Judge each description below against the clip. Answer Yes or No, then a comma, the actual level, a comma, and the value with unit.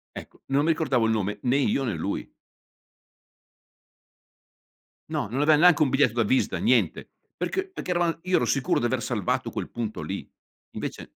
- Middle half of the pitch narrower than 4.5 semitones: No, average, 5.2 semitones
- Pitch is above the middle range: No, low, 135 Hz